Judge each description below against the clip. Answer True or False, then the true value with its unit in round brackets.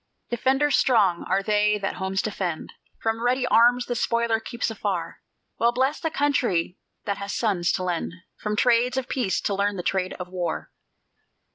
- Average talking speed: True (170 wpm)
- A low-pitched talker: False (215 Hz)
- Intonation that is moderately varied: True (4.4 semitones)